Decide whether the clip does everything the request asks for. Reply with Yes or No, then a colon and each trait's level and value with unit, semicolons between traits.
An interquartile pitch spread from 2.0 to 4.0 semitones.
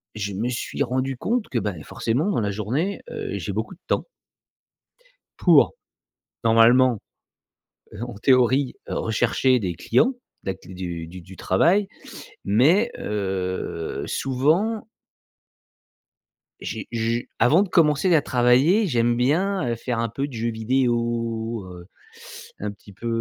No: average, 4.7 semitones